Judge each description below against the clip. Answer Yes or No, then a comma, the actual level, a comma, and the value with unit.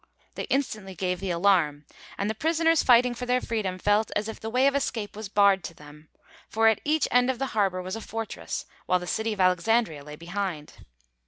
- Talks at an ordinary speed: No, fast, 215 wpm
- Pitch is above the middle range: Yes, high, 205 Hz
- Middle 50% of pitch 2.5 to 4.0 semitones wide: No, average, 4.5 semitones